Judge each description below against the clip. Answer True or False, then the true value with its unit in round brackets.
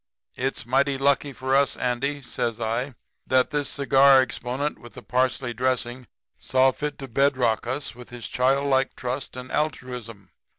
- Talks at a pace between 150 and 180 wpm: True (155 wpm)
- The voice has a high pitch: False (130 Hz)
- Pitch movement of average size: False (2.0 semitones)